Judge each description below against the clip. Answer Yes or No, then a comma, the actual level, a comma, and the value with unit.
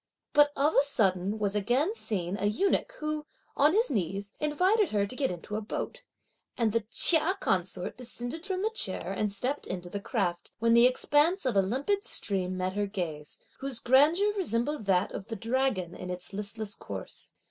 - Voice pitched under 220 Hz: No, high, 230 Hz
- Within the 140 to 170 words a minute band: No, average, 185 wpm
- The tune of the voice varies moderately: No, wide, 7.1 semitones